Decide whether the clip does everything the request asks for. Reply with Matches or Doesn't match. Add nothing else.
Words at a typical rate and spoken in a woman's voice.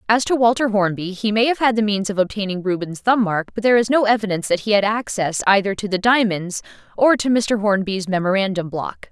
Doesn't match